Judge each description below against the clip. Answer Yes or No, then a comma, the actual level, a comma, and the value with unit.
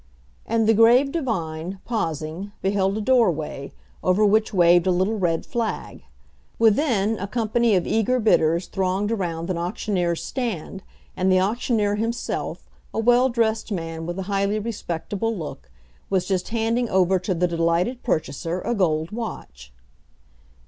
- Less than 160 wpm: Yes, average, 145 wpm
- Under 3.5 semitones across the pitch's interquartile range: No, average, 4.5 semitones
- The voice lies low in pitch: No, high, 195 Hz